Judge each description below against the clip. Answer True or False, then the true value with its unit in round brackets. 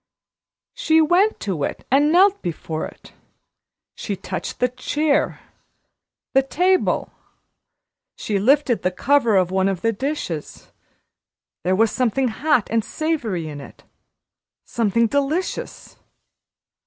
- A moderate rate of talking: False (115 wpm)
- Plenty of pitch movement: True (7.7 semitones)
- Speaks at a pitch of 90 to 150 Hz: False (245 Hz)